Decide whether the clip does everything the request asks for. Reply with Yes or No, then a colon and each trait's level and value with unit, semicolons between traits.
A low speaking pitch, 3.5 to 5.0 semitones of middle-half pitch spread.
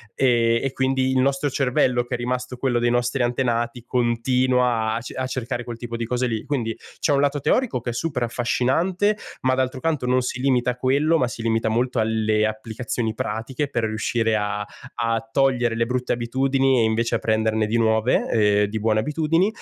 No: low, 120 Hz; narrow, 2.4 semitones